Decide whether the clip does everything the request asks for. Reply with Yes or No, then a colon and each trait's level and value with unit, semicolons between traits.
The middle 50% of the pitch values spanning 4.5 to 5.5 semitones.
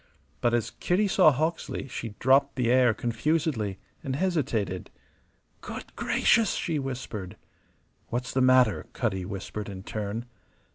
Yes: average, 5.0 semitones